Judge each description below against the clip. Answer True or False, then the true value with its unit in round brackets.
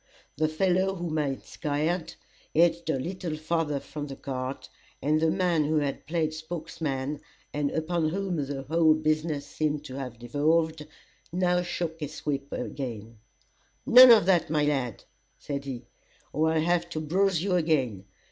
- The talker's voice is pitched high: False (155 Hz)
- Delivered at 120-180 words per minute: True (160 wpm)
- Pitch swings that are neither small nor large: True (3.0 semitones)